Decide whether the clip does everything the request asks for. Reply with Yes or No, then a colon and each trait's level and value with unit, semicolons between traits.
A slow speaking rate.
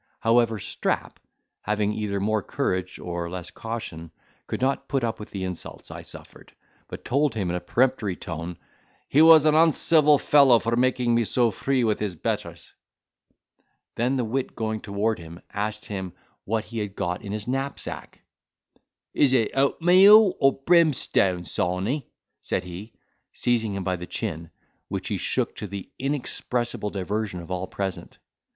No: average, 160 wpm